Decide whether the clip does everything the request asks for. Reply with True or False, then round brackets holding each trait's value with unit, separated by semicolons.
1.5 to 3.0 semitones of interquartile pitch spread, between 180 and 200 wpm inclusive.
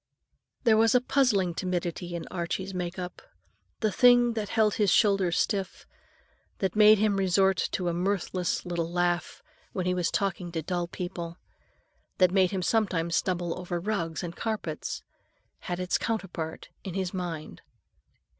False (2.6 semitones; 155 wpm)